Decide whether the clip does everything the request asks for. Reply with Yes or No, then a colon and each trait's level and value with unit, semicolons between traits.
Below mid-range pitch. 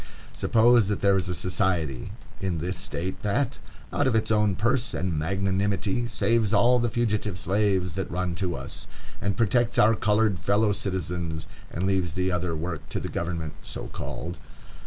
Yes: very low, 95 Hz